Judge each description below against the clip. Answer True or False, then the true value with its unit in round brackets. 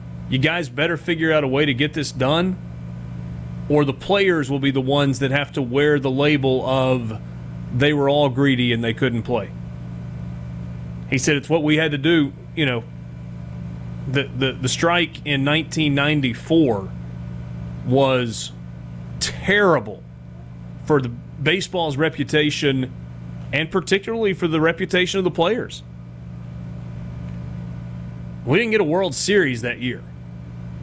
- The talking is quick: False (140 wpm)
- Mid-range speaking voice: False (130 Hz)